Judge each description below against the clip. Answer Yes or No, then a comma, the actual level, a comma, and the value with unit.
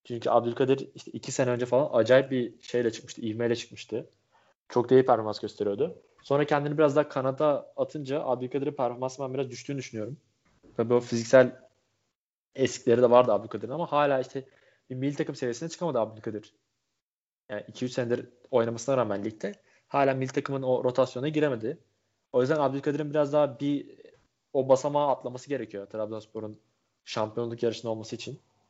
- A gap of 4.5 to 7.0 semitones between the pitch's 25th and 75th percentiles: No, average, 3.0 semitones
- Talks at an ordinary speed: No, fast, 150 wpm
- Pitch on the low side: Yes, low, 130 Hz